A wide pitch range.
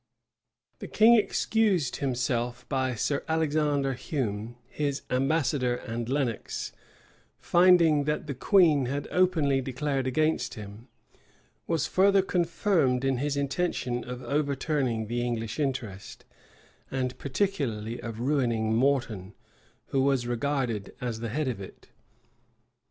No: average, 3.9 semitones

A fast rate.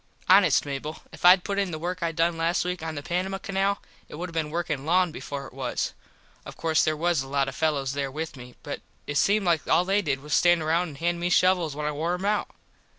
Yes: fast, 260 wpm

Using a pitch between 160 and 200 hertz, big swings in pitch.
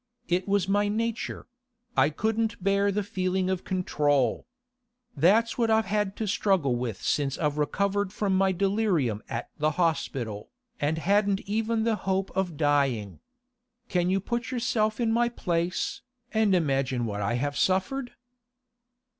Yes: high, 190 Hz; wide, 6.2 semitones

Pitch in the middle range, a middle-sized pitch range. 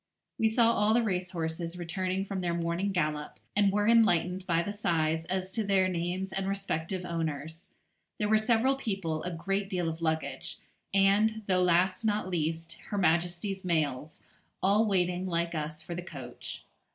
Yes: medium, 180 Hz; average, 3.1 semitones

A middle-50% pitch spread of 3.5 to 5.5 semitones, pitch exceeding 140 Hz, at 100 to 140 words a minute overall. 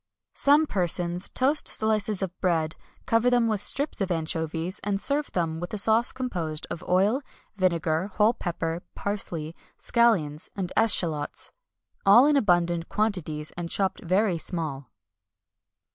Yes: average, 4.8 semitones; medium, 185 Hz; slow, 135 wpm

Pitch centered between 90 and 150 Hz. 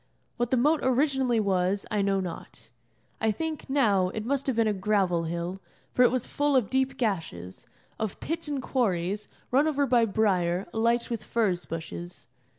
No: high, 220 Hz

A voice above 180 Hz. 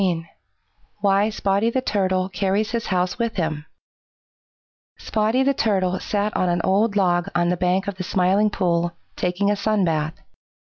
Yes: high, 190 Hz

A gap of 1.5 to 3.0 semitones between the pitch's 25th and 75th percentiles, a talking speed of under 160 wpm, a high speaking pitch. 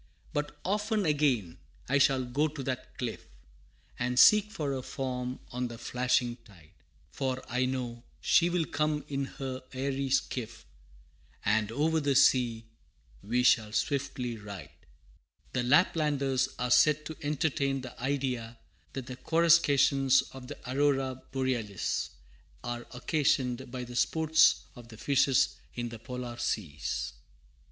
No: average, 2.7 semitones; average, 140 wpm; low, 130 Hz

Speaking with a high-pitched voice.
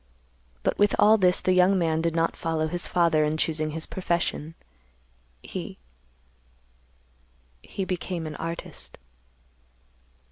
No: medium, 155 Hz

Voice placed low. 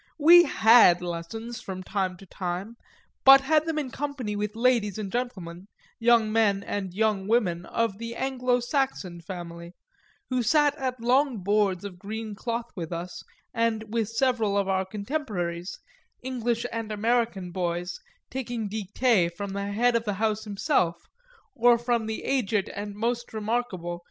No: high, 220 Hz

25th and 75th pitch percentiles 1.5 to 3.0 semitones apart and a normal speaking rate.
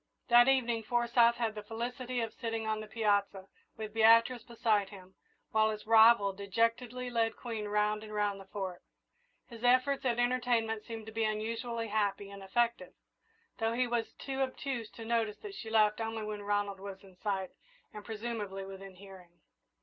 Yes: narrow, 2.4 semitones; average, 170 wpm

